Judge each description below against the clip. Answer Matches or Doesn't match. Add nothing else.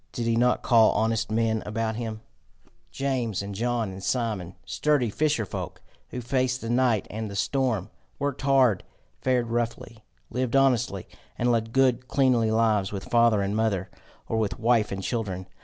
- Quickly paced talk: Doesn't match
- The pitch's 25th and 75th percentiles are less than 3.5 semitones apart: Matches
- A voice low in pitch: Matches